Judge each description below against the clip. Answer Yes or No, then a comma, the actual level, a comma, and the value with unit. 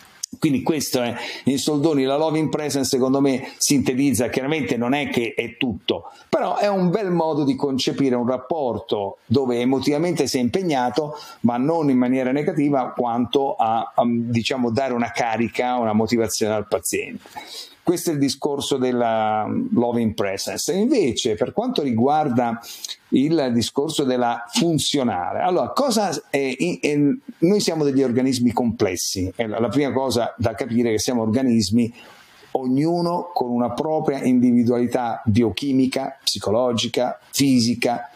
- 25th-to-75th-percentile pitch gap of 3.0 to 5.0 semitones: Yes, average, 3.4 semitones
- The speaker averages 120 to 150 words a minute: Yes, average, 145 wpm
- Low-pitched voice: Yes, low, 130 Hz